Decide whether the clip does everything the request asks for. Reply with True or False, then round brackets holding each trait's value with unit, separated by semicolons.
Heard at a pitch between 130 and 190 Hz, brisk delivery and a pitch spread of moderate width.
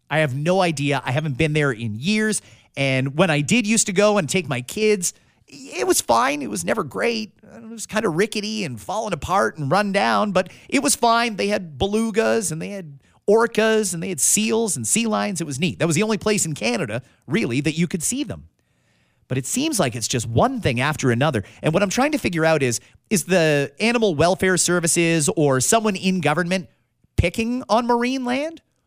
False (185 Hz; 215 wpm; 6.8 semitones)